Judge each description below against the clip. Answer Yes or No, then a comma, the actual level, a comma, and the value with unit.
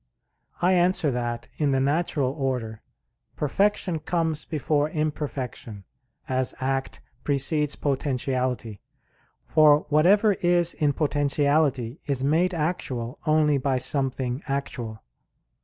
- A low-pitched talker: No, medium, 145 Hz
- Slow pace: Yes, slow, 105 wpm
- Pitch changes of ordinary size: Yes, average, 3.1 semitones